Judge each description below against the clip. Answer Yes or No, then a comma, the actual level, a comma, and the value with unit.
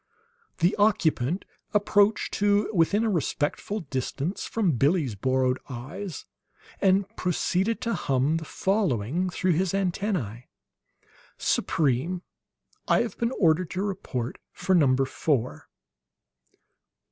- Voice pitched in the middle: Yes, medium, 175 Hz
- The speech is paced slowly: Yes, slow, 110 wpm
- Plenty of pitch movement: Yes, wide, 6.8 semitones